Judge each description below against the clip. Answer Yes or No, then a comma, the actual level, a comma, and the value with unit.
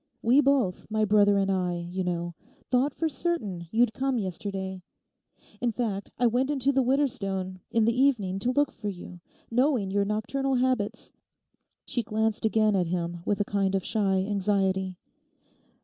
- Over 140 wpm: Yes, average, 165 wpm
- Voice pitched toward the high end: Yes, high, 210 Hz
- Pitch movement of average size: Yes, average, 4.6 semitones